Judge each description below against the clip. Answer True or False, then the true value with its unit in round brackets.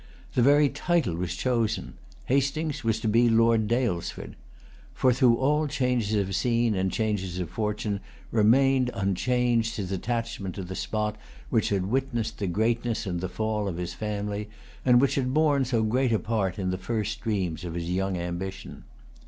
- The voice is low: True (110 Hz)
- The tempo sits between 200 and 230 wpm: False (170 wpm)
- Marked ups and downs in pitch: False (4.3 semitones)